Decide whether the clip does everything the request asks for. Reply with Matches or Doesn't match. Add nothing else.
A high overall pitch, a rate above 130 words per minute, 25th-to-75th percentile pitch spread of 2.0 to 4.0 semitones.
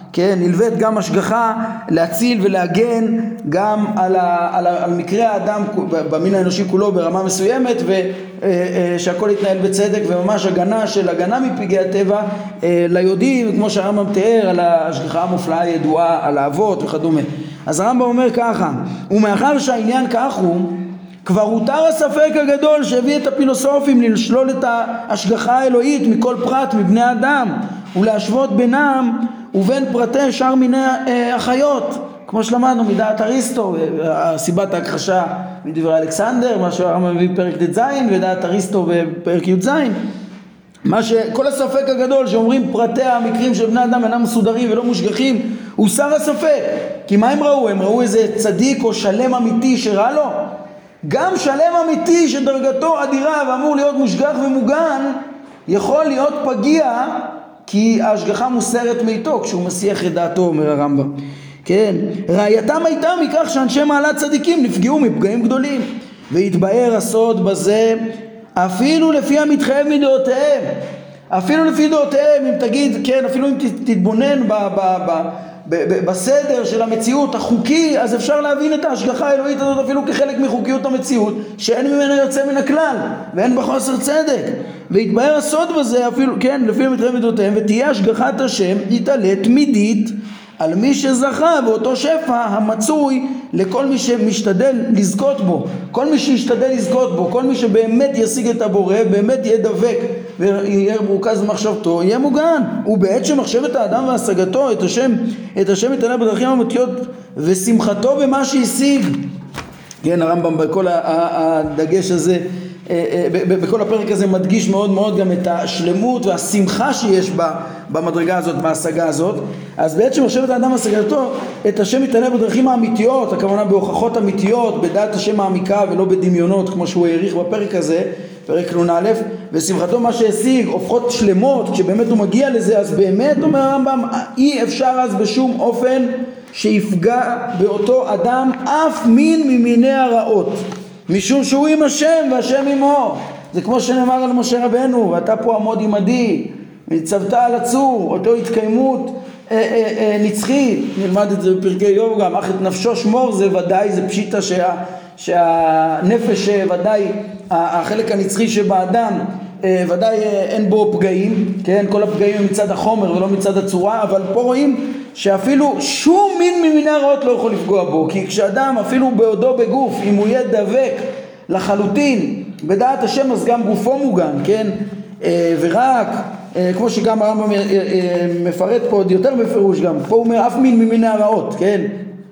Doesn't match